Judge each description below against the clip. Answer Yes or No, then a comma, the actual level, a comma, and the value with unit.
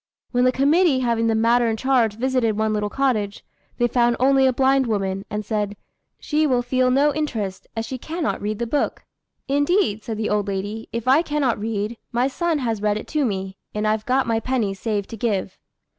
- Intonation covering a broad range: No, average, 3.9 semitones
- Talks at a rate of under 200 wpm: No, fast, 205 wpm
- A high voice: Yes, high, 235 Hz